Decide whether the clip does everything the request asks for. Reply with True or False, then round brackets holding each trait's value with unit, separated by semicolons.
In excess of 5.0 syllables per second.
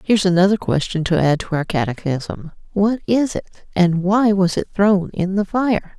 False (4.8 syllables/s)